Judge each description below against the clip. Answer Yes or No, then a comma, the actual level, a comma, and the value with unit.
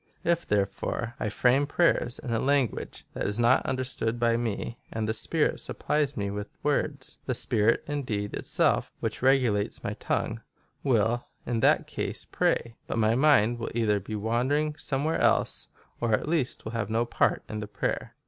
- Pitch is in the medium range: No, low, 120 Hz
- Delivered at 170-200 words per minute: Yes, average, 180 wpm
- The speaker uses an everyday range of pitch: Yes, average, 3.8 semitones